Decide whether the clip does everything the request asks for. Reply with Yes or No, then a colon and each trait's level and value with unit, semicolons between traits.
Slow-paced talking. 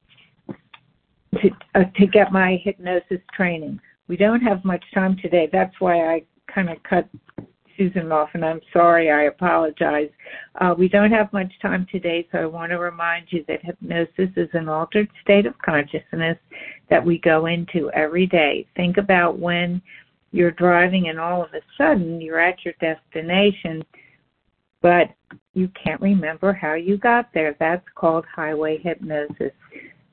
No: average, 155 wpm